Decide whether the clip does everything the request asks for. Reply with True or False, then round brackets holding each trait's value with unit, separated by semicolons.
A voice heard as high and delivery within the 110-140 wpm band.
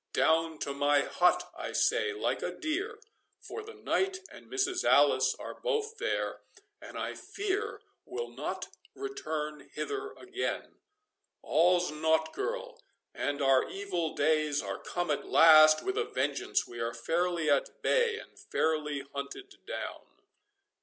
False (175 Hz; 135 wpm)